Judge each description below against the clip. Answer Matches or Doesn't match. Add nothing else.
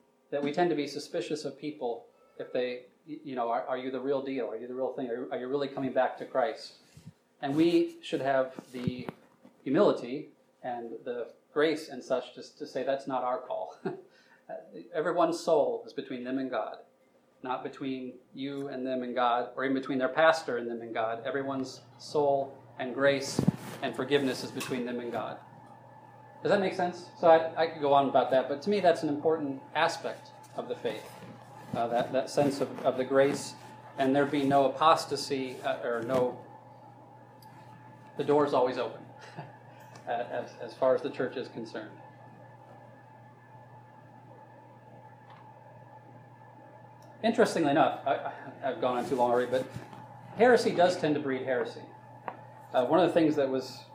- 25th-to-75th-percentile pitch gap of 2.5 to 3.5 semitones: Matches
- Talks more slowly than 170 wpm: Doesn't match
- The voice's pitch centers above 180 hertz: Doesn't match